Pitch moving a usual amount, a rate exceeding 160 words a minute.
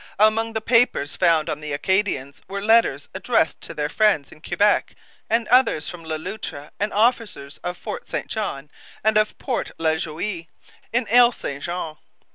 No: wide, 6.2 semitones; average, 170 wpm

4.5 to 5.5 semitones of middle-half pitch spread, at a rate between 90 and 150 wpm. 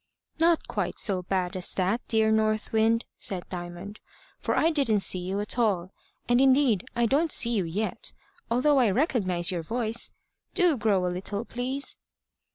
No: average, 4.9 semitones; average, 165 wpm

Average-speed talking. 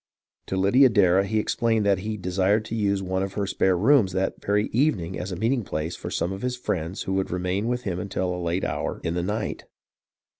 No: fast, 225 wpm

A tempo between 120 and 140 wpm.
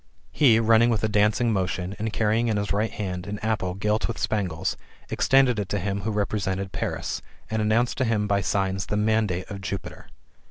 No: average, 195 wpm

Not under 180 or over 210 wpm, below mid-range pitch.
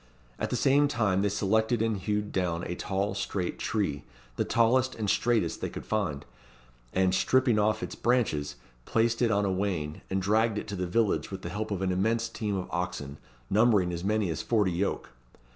Yes: average, 195 wpm; low, 100 Hz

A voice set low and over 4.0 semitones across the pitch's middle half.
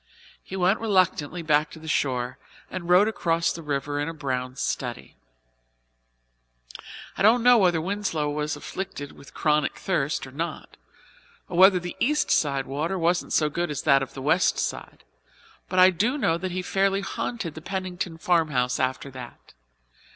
No: medium, 165 Hz; average, 4.4 semitones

